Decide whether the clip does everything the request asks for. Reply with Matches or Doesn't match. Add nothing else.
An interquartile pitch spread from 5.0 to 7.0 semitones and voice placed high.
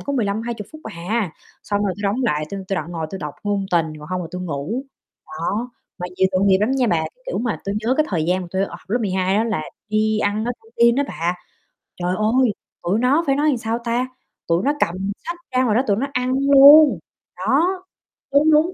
Matches